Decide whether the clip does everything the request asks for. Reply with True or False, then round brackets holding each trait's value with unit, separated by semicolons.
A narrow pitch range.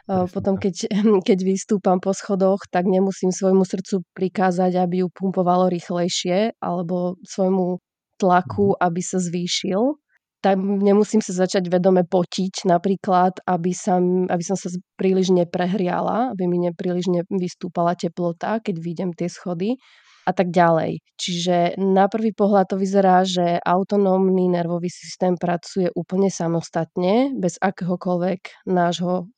True (1.5 semitones)